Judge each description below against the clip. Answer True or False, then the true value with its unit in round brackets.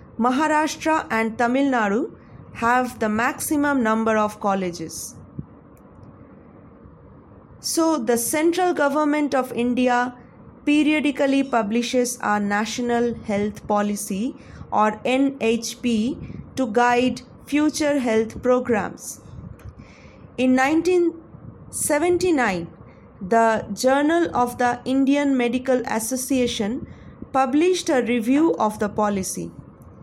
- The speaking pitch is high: True (250 Hz)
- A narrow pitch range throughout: False (4.2 semitones)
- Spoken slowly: True (90 wpm)